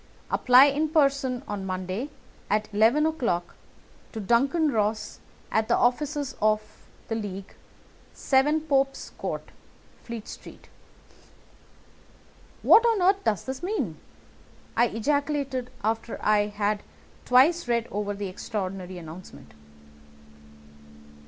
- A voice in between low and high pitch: No, high, 235 Hz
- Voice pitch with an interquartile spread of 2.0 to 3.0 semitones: No, wide, 5.4 semitones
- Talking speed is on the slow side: Yes, slow, 110 wpm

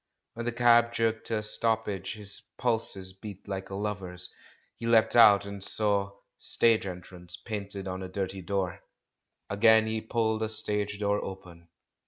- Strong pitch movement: No, narrow, 2.5 semitones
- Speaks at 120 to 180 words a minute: Yes, average, 160 wpm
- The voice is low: Yes, low, 105 Hz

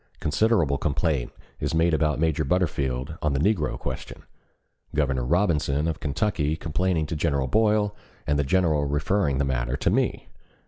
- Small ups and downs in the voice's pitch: No, average, 3.5 semitones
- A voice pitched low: Yes, very low, 75 Hz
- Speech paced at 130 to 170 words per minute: Yes, average, 150 wpm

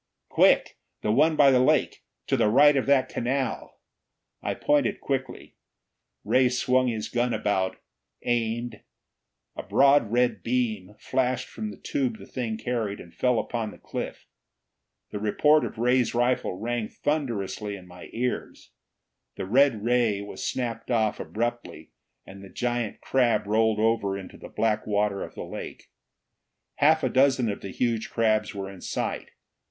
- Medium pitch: No, low, 120 Hz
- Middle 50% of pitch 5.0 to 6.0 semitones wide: No, average, 3.3 semitones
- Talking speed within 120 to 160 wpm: Yes, average, 155 wpm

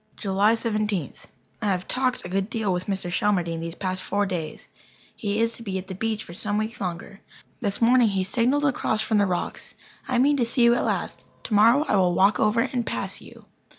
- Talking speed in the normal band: No, fast, 215 wpm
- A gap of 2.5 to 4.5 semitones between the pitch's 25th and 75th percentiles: Yes, average, 3.5 semitones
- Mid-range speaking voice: No, high, 210 Hz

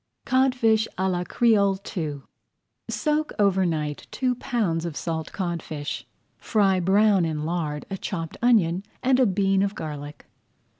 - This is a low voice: No, high, 190 Hz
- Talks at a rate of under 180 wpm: Yes, average, 140 wpm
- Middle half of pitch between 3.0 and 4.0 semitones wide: No, average, 5.1 semitones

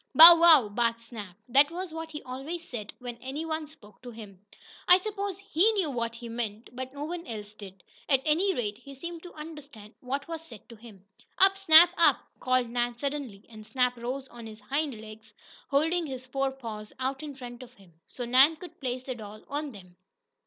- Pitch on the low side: No, very high, 260 Hz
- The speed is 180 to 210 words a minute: Yes, fast, 205 wpm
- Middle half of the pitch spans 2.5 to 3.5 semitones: No, wide, 5.4 semitones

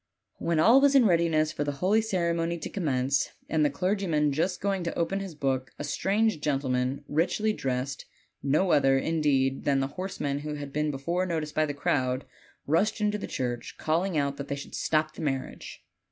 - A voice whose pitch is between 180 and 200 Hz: No, medium, 155 Hz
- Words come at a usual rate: Yes, average, 195 wpm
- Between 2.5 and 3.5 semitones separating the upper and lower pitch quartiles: No, average, 4.6 semitones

